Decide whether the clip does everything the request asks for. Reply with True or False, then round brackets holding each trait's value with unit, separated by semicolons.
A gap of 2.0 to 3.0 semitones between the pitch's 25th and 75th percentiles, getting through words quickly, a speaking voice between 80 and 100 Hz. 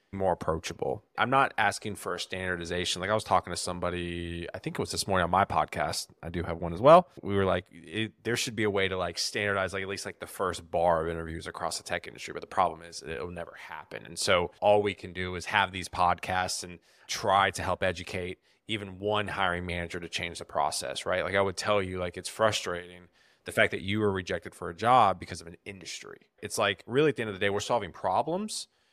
True (2.6 semitones; 245 wpm; 90 Hz)